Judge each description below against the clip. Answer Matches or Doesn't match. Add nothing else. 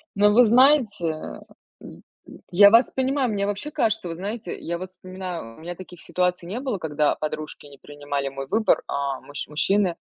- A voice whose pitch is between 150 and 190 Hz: Matches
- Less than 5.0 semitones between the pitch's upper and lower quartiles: Doesn't match